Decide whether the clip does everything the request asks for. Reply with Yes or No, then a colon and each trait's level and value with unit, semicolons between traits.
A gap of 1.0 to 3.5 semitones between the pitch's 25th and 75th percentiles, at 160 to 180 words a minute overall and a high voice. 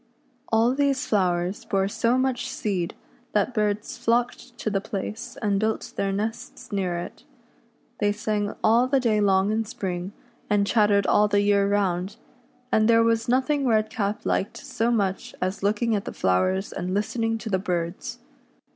Yes: average, 2.7 semitones; average, 165 wpm; high, 210 Hz